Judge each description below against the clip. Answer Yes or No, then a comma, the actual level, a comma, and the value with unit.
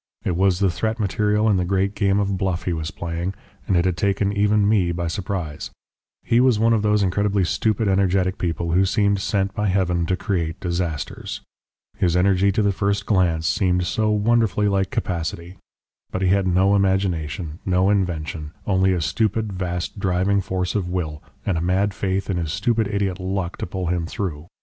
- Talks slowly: No, average, 190 wpm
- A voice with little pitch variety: Yes, narrow, 2.3 semitones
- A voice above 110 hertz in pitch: No, very low, 95 Hz